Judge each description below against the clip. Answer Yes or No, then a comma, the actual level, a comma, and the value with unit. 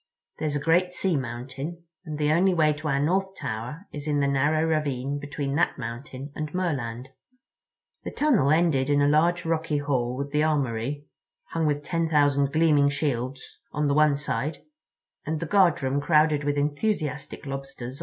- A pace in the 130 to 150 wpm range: No, average, 180 wpm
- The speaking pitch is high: No, medium, 145 Hz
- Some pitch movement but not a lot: No, narrow, 2.3 semitones